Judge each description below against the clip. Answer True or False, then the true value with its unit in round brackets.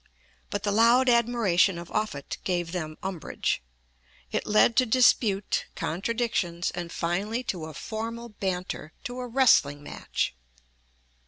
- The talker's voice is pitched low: False (205 Hz)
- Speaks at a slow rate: True (130 wpm)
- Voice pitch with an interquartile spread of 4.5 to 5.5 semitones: True (5.1 semitones)